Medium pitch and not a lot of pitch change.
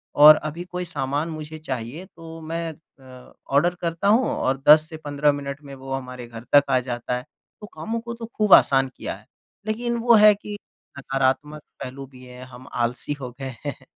No: medium, 145 Hz; average, 4.2 semitones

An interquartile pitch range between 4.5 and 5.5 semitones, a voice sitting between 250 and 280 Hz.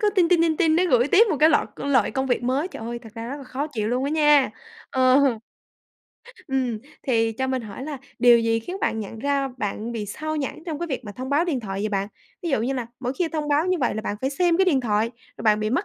Yes: average, 5.2 semitones; very high, 265 Hz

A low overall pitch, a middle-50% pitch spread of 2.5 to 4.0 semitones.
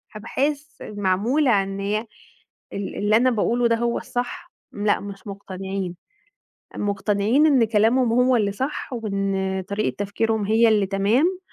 No: high, 215 Hz; average, 3.4 semitones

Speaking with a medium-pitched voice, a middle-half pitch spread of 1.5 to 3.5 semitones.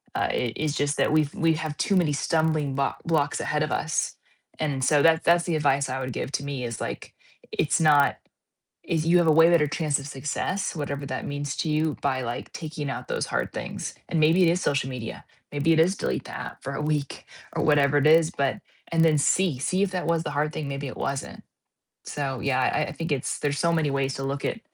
Yes: medium, 150 Hz; narrow, 2.6 semitones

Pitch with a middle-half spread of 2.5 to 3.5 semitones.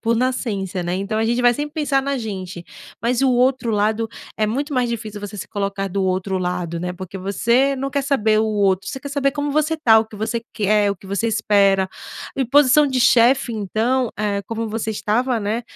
No: average, 4.4 semitones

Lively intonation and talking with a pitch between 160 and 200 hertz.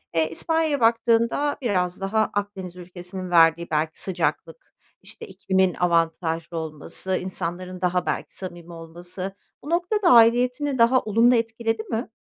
No: average, 5.0 semitones; high, 190 Hz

